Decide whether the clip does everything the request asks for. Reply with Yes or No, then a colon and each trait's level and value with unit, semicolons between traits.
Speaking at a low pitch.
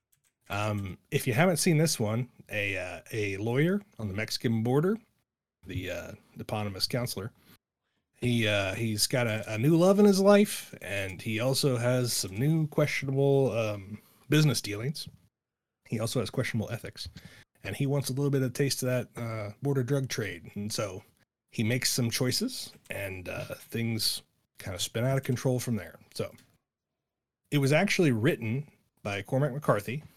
Yes: low, 120 Hz